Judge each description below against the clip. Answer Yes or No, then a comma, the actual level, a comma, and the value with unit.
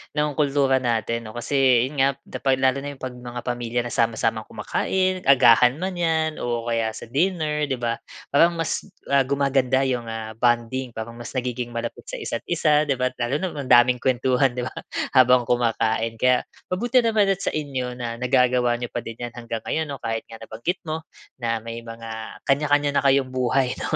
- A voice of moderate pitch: No, low, 125 Hz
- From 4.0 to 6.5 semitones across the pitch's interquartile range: No, average, 3.1 semitones